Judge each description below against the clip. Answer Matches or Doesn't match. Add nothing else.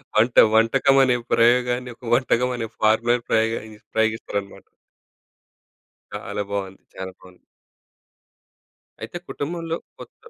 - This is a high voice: Doesn't match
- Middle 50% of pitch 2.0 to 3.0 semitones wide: Matches